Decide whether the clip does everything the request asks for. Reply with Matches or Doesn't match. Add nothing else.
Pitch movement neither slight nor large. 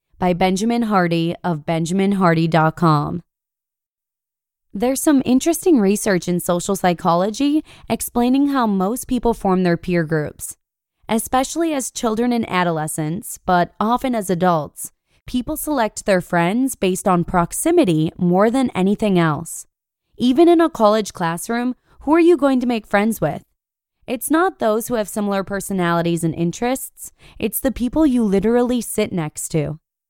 Doesn't match